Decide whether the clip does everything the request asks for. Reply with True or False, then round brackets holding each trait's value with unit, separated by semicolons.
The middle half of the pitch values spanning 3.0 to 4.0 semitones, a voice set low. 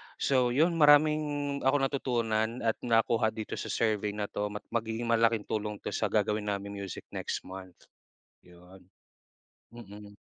True (3.5 semitones; 110 Hz)